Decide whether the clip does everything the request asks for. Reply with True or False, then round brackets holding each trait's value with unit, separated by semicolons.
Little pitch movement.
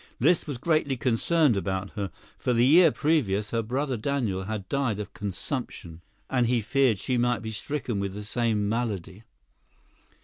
False (5.1 semitones)